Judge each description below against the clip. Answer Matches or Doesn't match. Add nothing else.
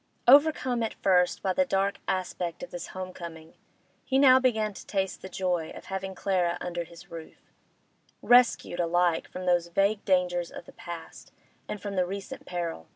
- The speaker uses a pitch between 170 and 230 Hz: Matches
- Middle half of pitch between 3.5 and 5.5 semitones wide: Doesn't match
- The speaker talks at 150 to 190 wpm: Matches